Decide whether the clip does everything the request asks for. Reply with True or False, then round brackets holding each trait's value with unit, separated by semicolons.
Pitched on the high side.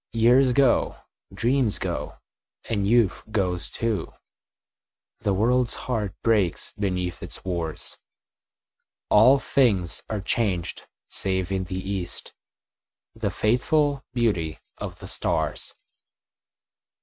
False (105 Hz)